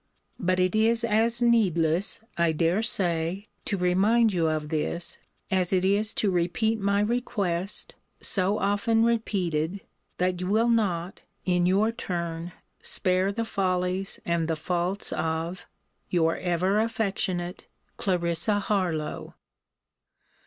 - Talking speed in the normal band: No, slow, 125 wpm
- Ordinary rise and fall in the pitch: Yes, average, 3.5 semitones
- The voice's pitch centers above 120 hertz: Yes, medium, 185 Hz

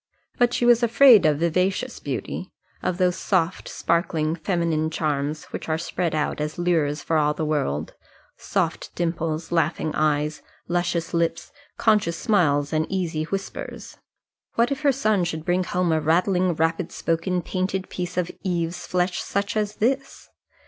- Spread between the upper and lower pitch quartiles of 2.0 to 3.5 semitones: Yes, average, 3.0 semitones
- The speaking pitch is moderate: Yes, medium, 170 Hz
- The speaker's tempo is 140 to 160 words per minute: Yes, average, 155 wpm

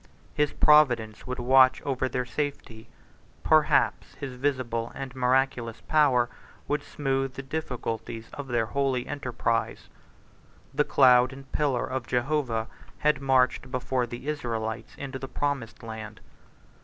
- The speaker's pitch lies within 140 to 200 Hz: No, low, 130 Hz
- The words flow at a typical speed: No, slow, 130 wpm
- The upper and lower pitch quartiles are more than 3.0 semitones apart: No, narrow, 2.5 semitones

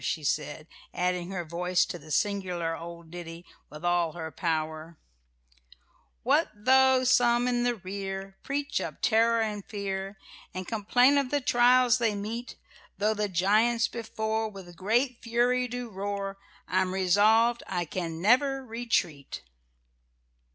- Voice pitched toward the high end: Yes, high, 205 Hz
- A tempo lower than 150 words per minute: Yes, slow, 135 wpm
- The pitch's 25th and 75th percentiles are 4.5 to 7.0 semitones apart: Yes, average, 5.3 semitones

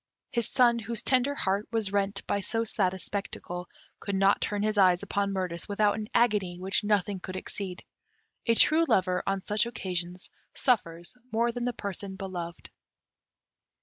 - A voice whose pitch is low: No, high, 200 Hz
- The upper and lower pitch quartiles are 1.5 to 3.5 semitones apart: Yes, average, 3.1 semitones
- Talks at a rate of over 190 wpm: No, average, 165 wpm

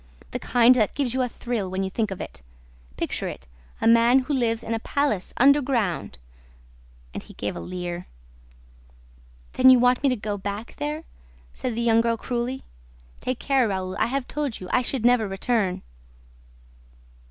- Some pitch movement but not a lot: Yes, average, 4.4 semitones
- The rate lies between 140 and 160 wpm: No, average, 175 wpm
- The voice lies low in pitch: No, high, 230 Hz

